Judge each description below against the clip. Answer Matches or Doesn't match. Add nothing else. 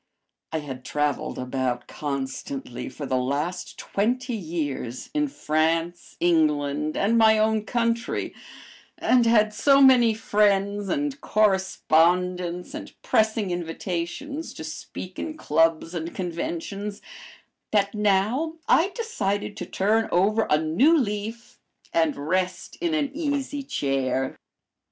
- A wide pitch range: Matches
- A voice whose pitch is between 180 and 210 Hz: Matches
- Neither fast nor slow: Doesn't match